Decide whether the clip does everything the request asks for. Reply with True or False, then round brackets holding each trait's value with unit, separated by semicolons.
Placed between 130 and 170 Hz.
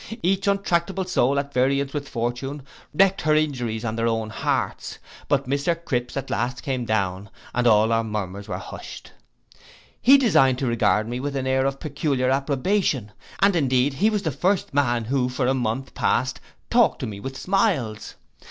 True (135 Hz)